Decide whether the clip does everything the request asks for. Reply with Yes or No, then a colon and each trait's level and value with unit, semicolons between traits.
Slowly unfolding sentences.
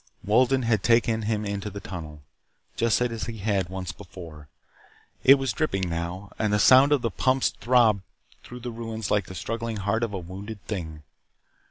No: average, 180 wpm